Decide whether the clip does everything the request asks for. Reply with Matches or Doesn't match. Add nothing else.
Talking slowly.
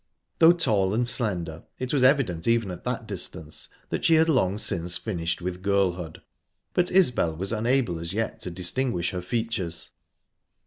Doesn't match